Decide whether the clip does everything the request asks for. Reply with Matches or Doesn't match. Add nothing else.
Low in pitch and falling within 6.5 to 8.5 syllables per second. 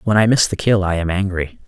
Doesn't match